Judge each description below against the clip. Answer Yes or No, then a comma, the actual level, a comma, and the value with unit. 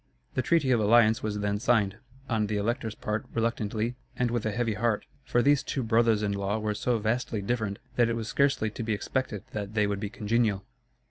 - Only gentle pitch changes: Yes, narrow, 2.3 semitones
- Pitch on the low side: Yes, low, 110 Hz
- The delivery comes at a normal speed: No, fast, 210 wpm